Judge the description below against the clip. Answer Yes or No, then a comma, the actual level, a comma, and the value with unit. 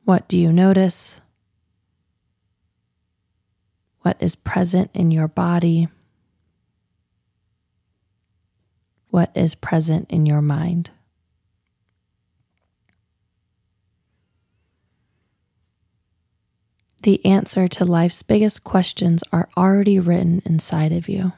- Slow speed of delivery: Yes, slow, 80 wpm